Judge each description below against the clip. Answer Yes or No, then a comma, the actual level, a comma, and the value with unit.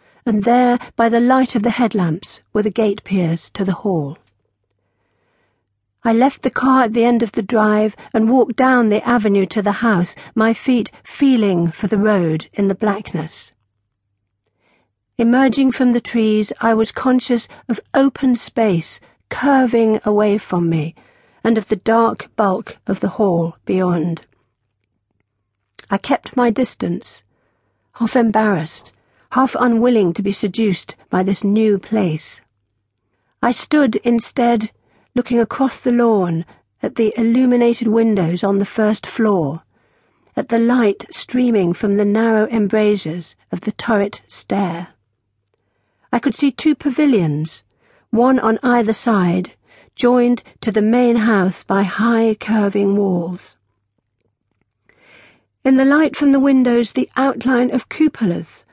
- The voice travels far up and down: Yes, wide, 6.2 semitones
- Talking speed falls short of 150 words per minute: Yes, average, 140 wpm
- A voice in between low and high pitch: No, high, 215 Hz